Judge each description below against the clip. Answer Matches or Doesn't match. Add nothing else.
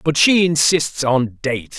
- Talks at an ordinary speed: Matches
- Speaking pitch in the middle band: Matches